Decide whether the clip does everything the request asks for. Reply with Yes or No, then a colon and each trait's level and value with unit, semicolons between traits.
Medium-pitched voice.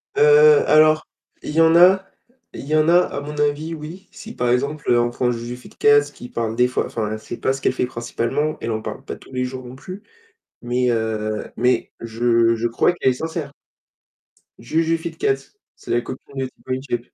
No: low, 130 Hz